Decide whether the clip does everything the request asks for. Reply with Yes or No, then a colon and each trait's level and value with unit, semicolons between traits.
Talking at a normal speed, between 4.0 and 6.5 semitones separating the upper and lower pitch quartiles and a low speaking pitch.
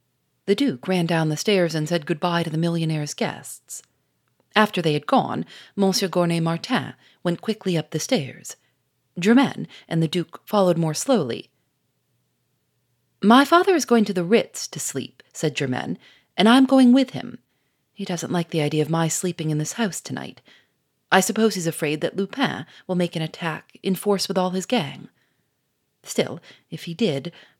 No: average, 175 wpm; average, 4.5 semitones; medium, 175 Hz